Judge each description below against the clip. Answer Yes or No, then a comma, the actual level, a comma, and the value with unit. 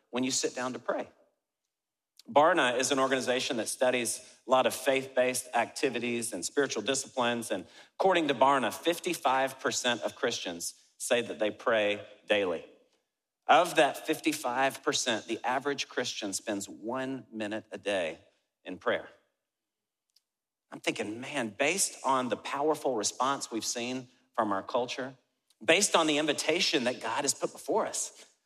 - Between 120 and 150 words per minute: Yes, average, 145 wpm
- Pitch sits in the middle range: No, low, 130 Hz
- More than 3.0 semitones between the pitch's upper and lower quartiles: No, average, 2.7 semitones